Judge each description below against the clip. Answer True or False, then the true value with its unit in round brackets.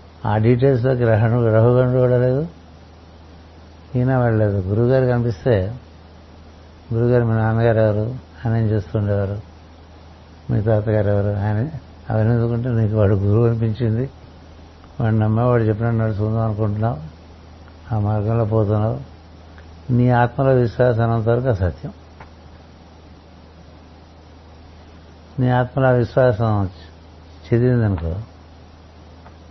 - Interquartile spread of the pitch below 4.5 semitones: False (6.1 semitones)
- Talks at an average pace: True (90 wpm)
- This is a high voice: False (105 Hz)